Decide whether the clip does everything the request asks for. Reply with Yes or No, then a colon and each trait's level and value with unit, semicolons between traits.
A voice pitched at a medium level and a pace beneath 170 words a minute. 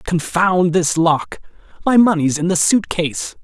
Yes: medium, 170 Hz; average, 140 wpm